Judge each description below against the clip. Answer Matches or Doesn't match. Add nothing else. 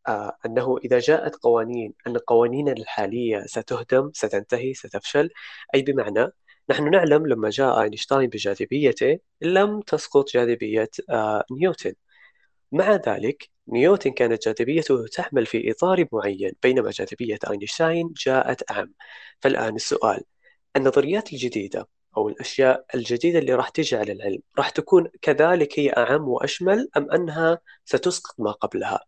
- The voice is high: Doesn't match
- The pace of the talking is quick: Doesn't match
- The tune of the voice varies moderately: Doesn't match